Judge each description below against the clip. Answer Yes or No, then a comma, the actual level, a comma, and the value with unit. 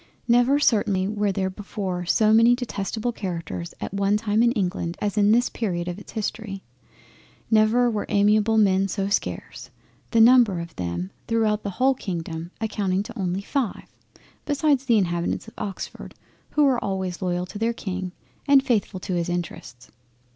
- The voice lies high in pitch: Yes, high, 205 Hz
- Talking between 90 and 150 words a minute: No, average, 165 wpm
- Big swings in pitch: No, average, 3.7 semitones